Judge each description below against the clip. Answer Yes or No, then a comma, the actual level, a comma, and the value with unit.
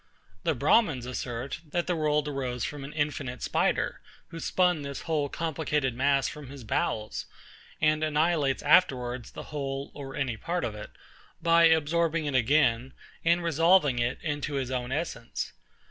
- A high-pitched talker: No, medium, 145 Hz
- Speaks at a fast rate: No, average, 155 wpm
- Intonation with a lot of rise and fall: No, average, 3.7 semitones